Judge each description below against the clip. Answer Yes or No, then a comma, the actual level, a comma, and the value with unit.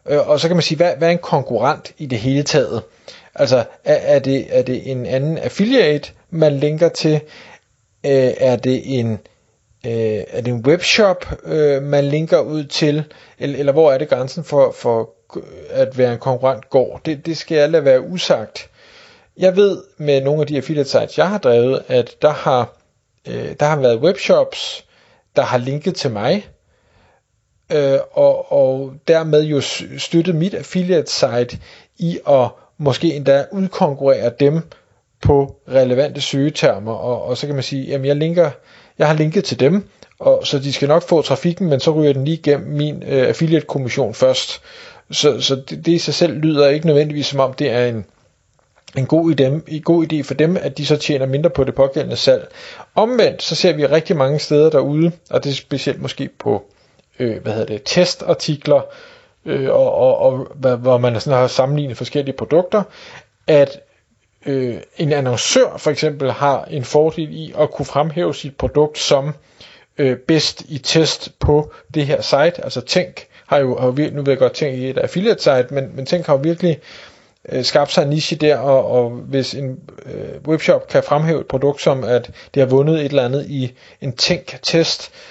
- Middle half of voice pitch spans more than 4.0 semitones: No, average, 3.6 semitones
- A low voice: No, medium, 145 Hz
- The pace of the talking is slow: No, average, 185 wpm